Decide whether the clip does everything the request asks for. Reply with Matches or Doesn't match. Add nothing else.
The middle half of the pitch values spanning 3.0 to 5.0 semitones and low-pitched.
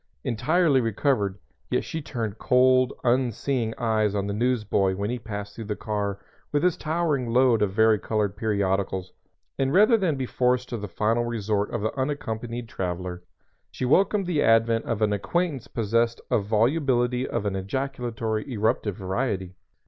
Matches